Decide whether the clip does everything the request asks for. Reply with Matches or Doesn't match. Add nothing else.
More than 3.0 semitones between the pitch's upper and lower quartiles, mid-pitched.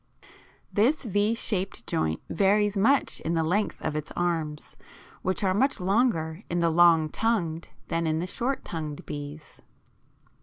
Matches